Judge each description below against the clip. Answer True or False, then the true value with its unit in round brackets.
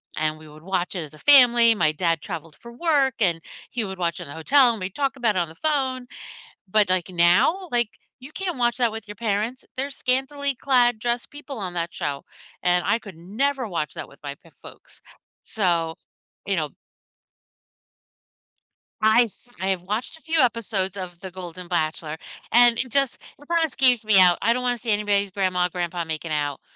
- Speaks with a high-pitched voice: True (205 Hz)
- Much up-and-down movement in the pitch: True (6.2 semitones)